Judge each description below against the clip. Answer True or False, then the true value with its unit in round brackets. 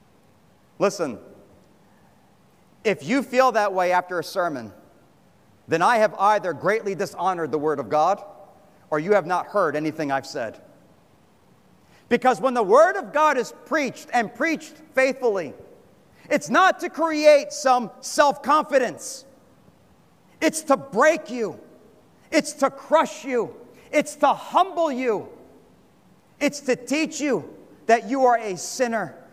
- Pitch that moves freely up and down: True (6.5 semitones)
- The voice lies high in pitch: True (255 Hz)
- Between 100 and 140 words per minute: True (135 wpm)